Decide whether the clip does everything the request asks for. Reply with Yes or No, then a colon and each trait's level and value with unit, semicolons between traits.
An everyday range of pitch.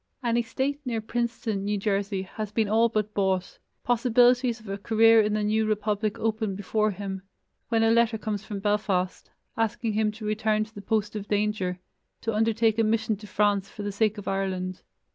No: narrow, 1.8 semitones